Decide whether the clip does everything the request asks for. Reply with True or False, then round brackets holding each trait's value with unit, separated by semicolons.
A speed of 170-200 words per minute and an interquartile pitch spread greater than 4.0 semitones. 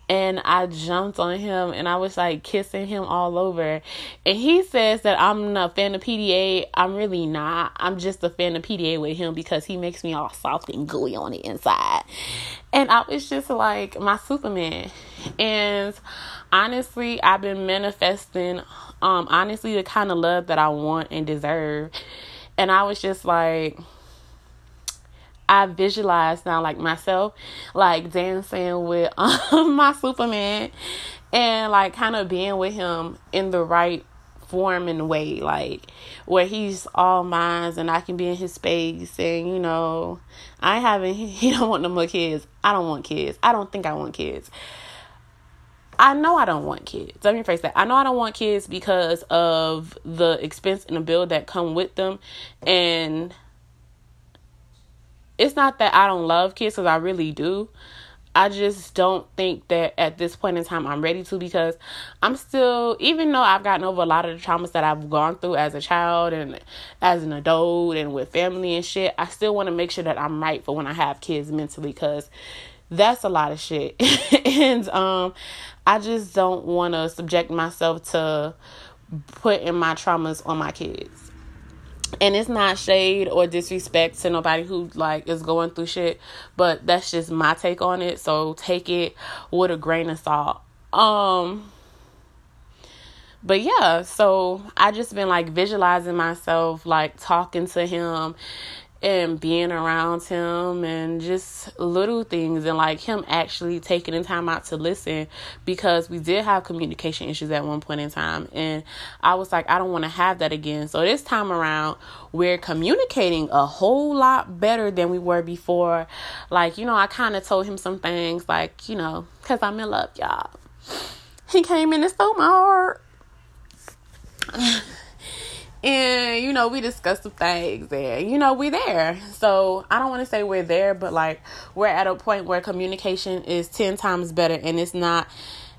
False (180 wpm; 3.3 semitones)